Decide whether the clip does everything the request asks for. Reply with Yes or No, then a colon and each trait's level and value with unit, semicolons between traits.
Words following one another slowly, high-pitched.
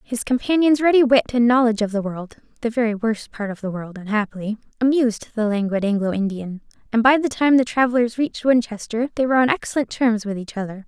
No: average, 200 wpm; high, 230 Hz